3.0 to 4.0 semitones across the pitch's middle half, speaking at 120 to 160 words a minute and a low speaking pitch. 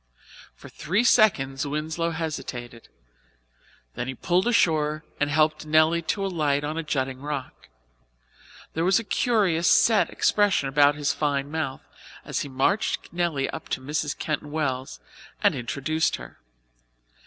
No: average, 3.3 semitones; average, 140 wpm; medium, 155 Hz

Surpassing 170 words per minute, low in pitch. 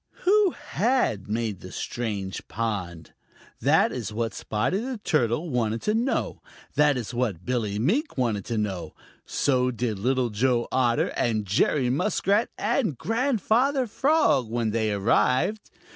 No: average, 140 wpm; low, 125 Hz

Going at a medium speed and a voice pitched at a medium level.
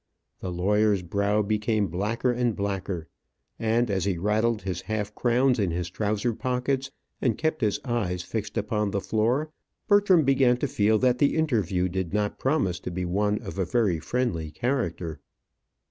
No: average, 165 wpm; low, 105 Hz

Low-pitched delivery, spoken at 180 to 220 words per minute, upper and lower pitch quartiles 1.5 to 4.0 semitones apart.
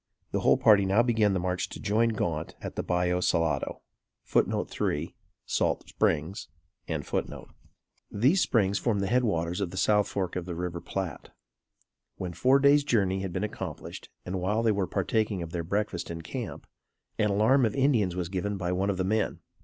Yes: very low, 95 Hz; average, 185 wpm; average, 3.4 semitones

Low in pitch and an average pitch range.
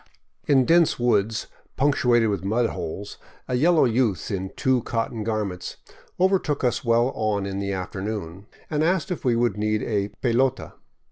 Yes: low, 115 Hz; average, 4.4 semitones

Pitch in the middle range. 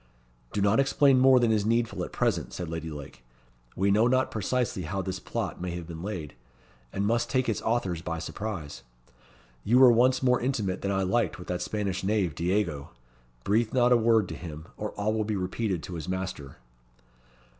No: low, 100 Hz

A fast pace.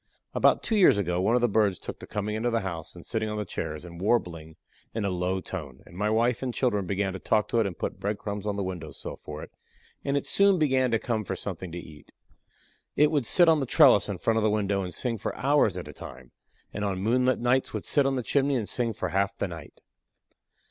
Yes: fast, 255 wpm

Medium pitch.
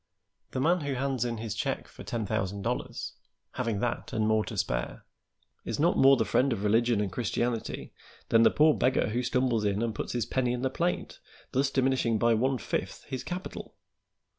No: low, 120 Hz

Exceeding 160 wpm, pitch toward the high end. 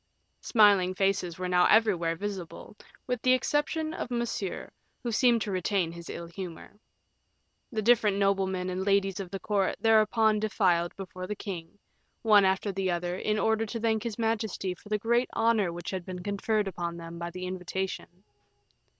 Yes: average, 170 wpm; high, 195 Hz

